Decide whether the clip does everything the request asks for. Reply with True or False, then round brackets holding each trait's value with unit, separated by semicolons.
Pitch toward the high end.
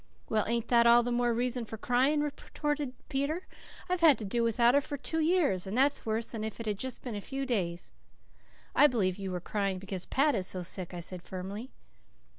True (235 Hz)